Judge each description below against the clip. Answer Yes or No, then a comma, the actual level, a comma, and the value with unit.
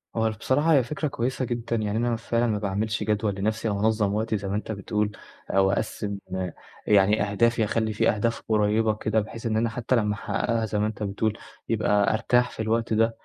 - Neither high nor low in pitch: No, low, 110 Hz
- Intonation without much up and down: Yes, narrow, 1.8 semitones